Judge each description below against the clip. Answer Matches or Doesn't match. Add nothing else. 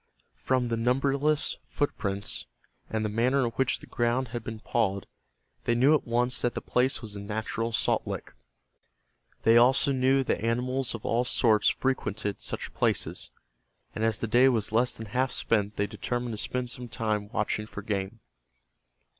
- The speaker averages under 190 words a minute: Matches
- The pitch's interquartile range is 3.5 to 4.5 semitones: Doesn't match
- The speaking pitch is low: Matches